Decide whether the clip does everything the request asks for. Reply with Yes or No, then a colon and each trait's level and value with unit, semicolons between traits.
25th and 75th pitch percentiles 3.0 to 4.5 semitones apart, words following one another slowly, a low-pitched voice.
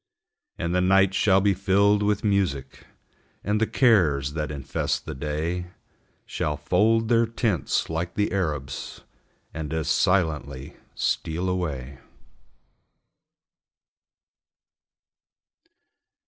No: average, 5.1 semitones; slow, 100 wpm; very low, 90 Hz